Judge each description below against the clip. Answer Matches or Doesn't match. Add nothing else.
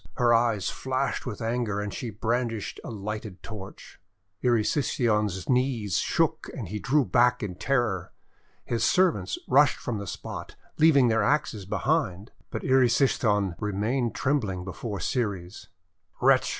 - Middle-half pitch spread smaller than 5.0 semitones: Matches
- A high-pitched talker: Doesn't match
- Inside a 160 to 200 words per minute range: Doesn't match